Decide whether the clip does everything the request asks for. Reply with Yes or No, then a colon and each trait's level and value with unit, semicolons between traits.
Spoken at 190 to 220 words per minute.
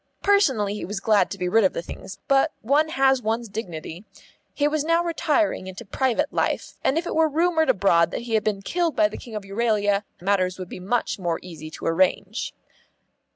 Yes: fast, 205 wpm